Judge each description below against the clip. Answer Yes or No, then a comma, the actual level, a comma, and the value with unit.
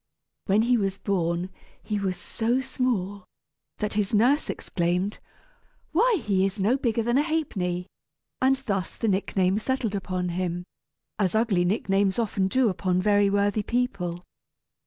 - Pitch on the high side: Yes, high, 200 Hz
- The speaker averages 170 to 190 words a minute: No, average, 145 wpm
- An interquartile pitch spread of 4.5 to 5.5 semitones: No, average, 3.9 semitones